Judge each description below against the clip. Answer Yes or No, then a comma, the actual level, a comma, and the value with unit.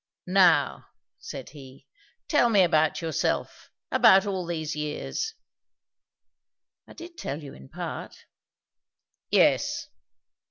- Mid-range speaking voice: Yes, medium, 165 Hz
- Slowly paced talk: Yes, slow, 105 wpm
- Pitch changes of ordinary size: Yes, average, 4.5 semitones